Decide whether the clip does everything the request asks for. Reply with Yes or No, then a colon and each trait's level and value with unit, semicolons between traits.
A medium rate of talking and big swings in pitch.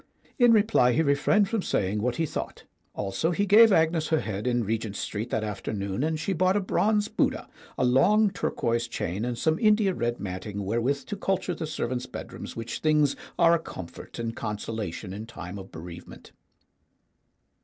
Yes: average, 175 wpm; wide, 8.5 semitones